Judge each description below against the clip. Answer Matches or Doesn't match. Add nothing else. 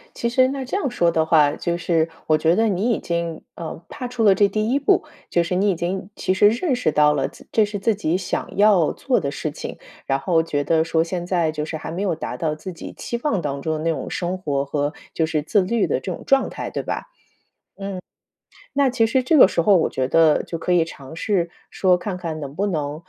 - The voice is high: Doesn't match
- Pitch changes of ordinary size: Matches